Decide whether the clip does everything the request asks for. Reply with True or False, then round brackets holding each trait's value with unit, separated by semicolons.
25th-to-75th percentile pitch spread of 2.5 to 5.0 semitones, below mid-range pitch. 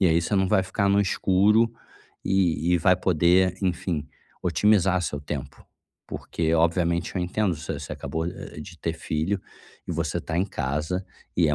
True (2.9 semitones; 90 Hz)